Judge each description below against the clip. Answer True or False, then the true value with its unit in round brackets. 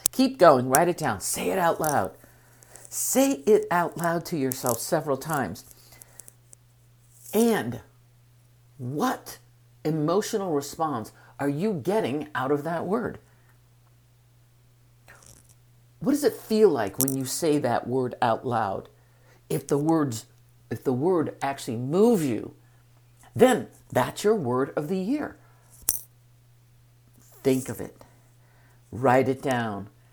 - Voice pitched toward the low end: True (125 Hz)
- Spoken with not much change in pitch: False (4.5 semitones)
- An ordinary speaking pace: False (125 wpm)